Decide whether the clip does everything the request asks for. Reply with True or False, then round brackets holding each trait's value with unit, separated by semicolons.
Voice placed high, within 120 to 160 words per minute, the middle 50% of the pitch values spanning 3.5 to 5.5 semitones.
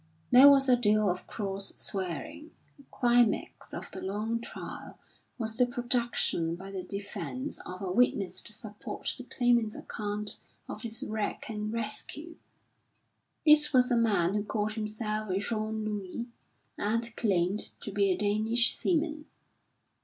False (215 Hz; 145 wpm; 3.0 semitones)